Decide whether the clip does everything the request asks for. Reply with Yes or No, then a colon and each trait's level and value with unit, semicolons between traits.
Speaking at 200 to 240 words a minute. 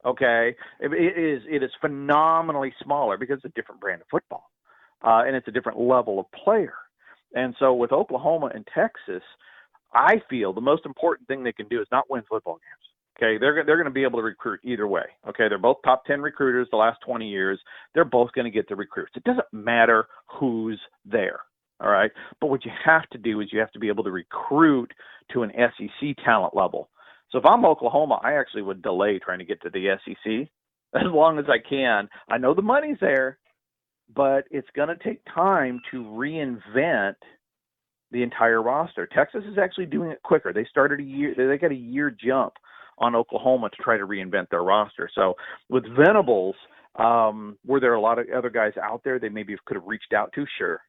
Yes: fast, 205 wpm